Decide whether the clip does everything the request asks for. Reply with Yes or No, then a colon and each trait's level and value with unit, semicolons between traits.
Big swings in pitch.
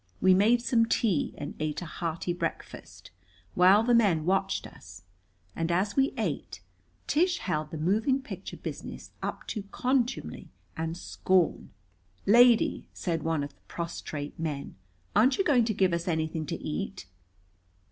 Yes: wide, 6.2 semitones